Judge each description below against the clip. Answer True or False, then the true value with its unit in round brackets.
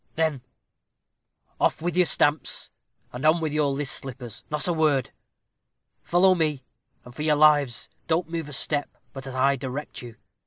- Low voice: False (145 Hz)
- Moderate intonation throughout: True (3.0 semitones)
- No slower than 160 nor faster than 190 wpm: True (165 wpm)